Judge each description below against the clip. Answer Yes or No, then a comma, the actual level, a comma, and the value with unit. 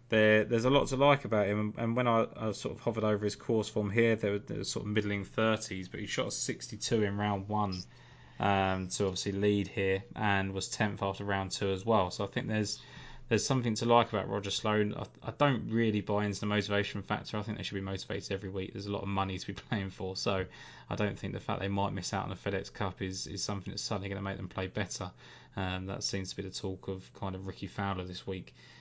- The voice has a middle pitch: No, low, 100 Hz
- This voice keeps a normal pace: No, fast, 255 wpm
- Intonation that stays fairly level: Yes, narrow, 2.0 semitones